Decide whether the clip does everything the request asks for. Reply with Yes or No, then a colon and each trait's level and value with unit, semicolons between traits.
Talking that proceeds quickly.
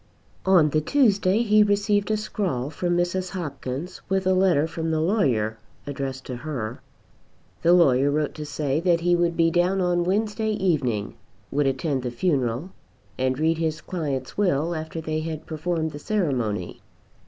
No: average, 165 wpm